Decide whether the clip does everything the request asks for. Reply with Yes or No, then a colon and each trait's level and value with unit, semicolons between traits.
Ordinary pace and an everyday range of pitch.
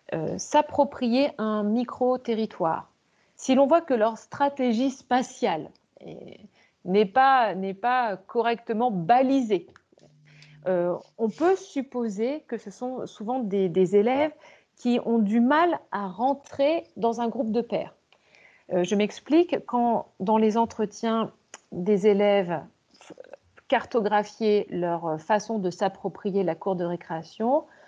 No: slow, 125 wpm; average, 4.3 semitones